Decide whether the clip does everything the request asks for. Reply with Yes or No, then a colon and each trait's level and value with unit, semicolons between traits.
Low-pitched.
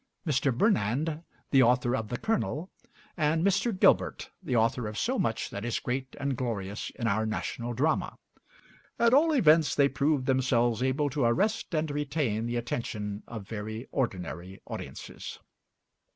Yes: low, 130 Hz